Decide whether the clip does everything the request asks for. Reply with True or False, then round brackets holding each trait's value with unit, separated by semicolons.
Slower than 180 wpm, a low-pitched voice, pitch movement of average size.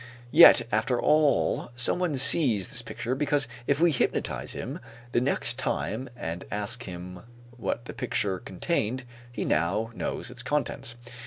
True (145 wpm; 120 Hz; 4.8 semitones)